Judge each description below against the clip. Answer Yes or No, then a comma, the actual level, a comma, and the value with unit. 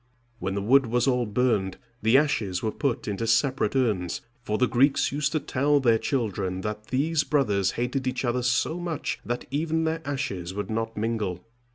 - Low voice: Yes, low, 120 Hz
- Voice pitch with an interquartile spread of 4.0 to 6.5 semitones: Yes, average, 4.7 semitones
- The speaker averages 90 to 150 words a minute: No, average, 185 wpm